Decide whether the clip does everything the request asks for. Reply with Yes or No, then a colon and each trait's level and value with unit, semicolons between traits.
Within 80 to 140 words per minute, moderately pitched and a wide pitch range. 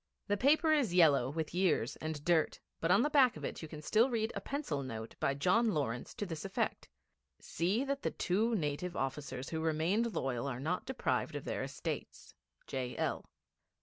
No: average, 185 wpm; medium, 165 Hz; wide, 7.6 semitones